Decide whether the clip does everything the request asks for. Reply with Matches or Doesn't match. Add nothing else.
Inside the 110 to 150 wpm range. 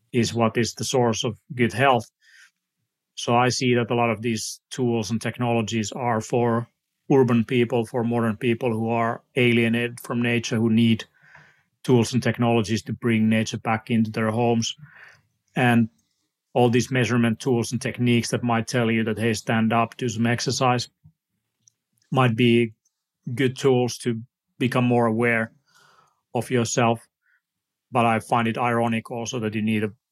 Doesn't match